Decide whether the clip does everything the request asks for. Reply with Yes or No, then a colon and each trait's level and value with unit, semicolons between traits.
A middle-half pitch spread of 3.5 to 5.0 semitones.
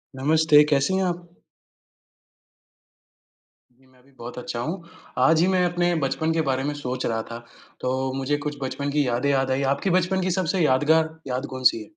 Yes: average, 4.0 semitones